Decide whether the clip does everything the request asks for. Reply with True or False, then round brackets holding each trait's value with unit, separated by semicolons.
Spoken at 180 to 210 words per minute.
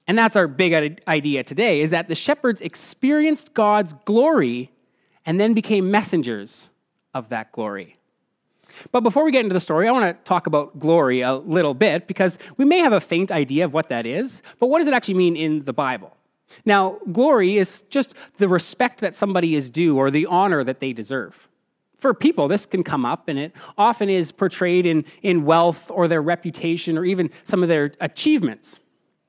True (195 wpm)